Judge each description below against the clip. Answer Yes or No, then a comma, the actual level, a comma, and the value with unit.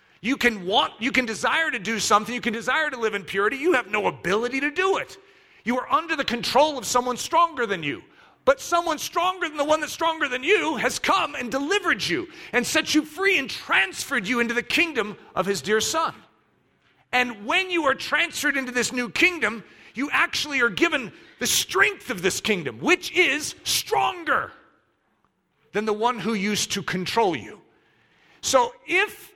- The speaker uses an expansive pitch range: Yes, wide, 6.5 semitones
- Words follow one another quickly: No, average, 190 wpm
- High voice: Yes, very high, 275 Hz